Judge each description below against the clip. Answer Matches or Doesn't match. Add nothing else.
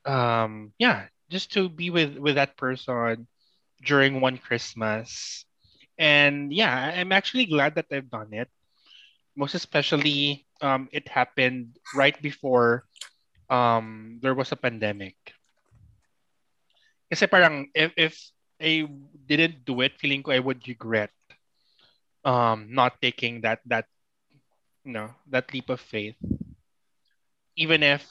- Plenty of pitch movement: Doesn't match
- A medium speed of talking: Matches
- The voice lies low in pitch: Matches